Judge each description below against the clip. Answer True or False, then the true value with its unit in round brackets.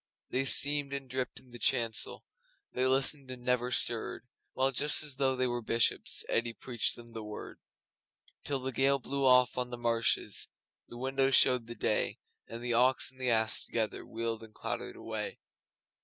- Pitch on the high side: False (125 Hz)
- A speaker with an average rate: True (185 wpm)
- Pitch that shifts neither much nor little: False (2.2 semitones)